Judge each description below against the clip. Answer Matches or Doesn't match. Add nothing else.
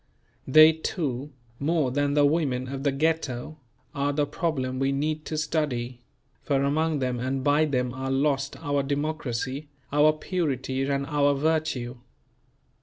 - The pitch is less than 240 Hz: Matches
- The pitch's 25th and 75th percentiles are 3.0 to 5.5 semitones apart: Doesn't match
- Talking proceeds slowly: Doesn't match